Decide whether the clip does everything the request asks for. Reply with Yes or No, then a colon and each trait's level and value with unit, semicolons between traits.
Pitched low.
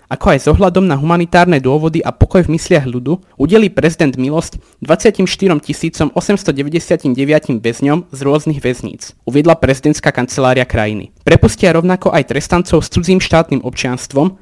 No: medium, 155 Hz